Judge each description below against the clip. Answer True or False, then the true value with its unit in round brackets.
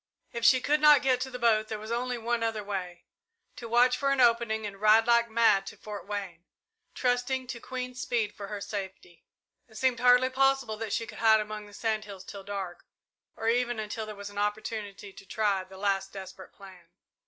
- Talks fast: True (210 wpm)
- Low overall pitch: False (220 Hz)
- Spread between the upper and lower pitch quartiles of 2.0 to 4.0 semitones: True (3.3 semitones)